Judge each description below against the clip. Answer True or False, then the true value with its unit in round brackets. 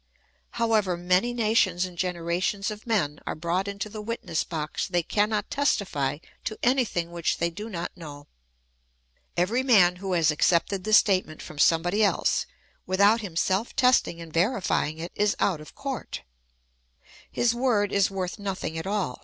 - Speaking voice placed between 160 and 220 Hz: True (190 Hz)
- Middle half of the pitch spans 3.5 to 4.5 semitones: True (4.0 semitones)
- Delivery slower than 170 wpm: True (155 wpm)